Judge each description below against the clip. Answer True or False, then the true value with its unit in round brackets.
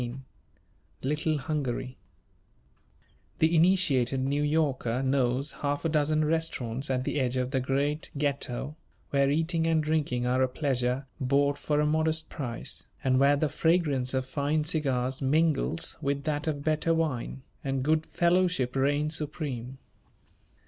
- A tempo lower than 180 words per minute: True (140 wpm)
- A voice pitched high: False (145 Hz)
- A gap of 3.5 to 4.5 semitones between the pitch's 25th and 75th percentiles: False (3.0 semitones)